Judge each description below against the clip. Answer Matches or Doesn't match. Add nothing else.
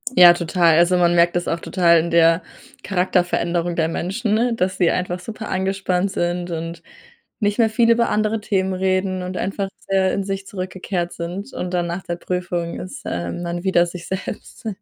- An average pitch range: Doesn't match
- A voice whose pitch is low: Doesn't match